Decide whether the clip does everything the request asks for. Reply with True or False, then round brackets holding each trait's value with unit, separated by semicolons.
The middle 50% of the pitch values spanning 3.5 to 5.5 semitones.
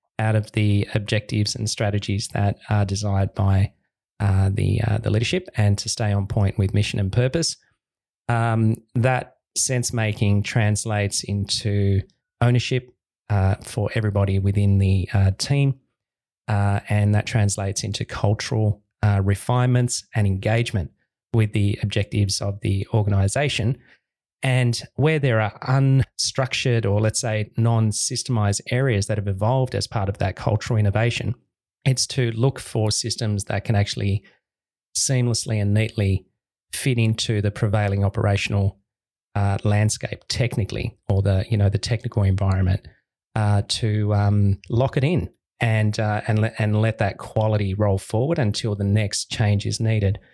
False (2.8 semitones)